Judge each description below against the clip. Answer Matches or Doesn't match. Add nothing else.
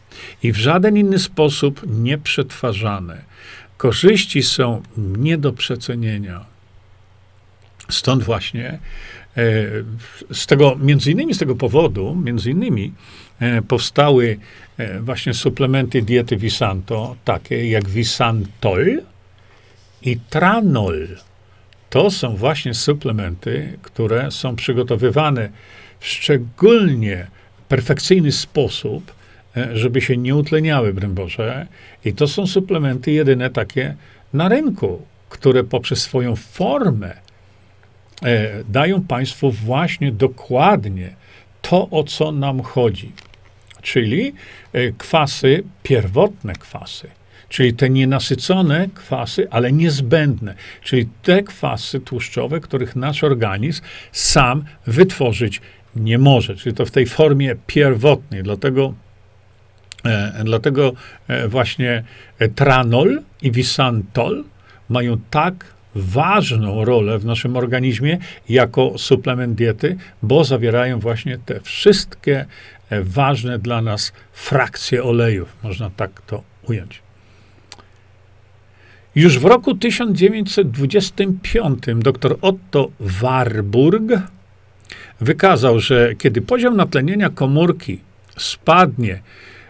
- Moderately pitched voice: Doesn't match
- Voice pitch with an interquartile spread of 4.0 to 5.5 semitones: Matches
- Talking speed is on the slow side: Matches